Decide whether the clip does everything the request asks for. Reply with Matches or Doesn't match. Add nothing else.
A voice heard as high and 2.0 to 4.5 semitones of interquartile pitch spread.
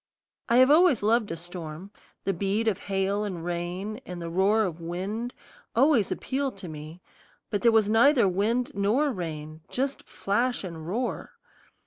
Doesn't match